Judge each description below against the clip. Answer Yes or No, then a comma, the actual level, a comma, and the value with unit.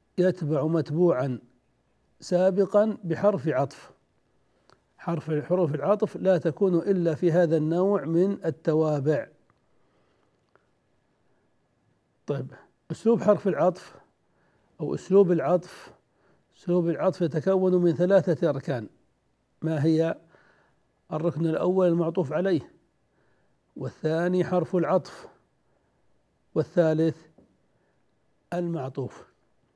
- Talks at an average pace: Yes, average, 80 wpm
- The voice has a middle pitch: Yes, medium, 170 Hz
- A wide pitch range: No, narrow, 2.5 semitones